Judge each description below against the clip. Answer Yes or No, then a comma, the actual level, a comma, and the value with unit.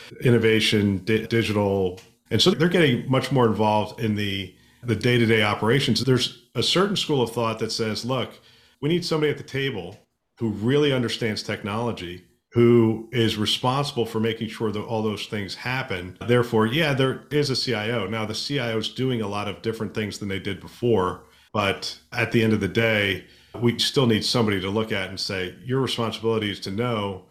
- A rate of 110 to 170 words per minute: No, average, 190 wpm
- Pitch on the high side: No, low, 115 Hz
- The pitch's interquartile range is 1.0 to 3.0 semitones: Yes, narrow, 2.6 semitones